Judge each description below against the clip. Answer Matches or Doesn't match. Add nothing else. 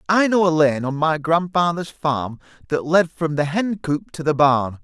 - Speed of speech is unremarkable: Doesn't match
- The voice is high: Doesn't match